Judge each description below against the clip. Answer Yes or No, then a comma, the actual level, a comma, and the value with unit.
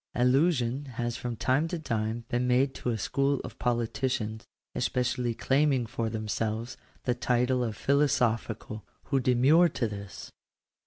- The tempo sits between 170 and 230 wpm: No, average, 150 wpm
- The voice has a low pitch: Yes, low, 125 Hz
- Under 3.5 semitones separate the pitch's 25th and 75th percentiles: Yes, average, 2.7 semitones